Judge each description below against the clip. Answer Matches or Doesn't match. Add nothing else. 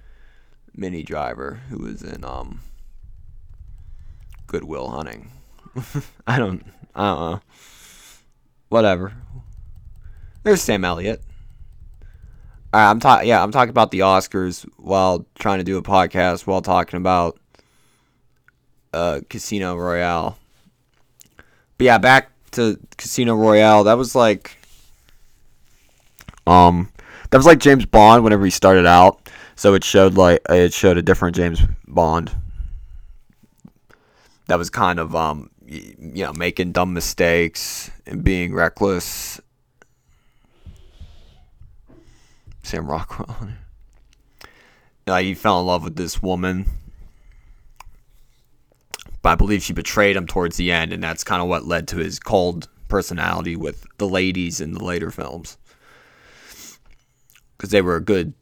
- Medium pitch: Doesn't match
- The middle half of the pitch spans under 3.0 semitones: Doesn't match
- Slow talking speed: Matches